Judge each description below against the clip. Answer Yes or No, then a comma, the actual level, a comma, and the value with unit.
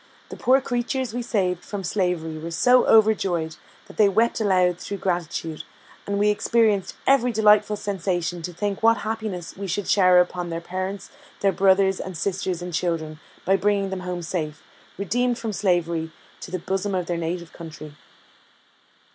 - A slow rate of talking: No, average, 165 wpm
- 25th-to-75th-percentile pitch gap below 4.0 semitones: Yes, average, 3.2 semitones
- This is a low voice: No, high, 190 Hz